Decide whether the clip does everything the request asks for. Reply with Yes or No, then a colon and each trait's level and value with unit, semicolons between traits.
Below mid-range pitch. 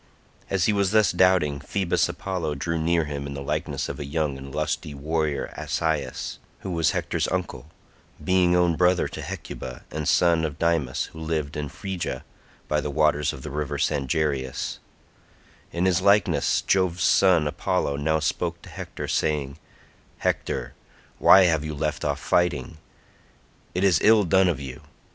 Yes: very low, 80 Hz